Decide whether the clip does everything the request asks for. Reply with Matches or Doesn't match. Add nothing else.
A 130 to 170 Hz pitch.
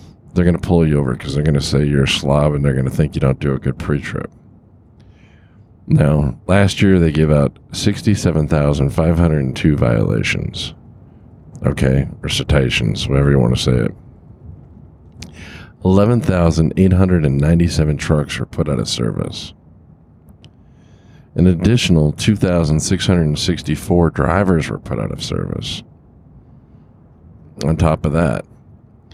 Doesn't match